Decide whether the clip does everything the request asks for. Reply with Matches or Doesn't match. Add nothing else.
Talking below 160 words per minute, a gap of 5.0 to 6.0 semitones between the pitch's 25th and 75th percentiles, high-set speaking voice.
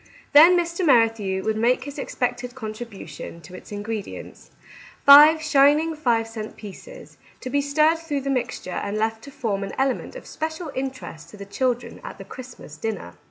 Doesn't match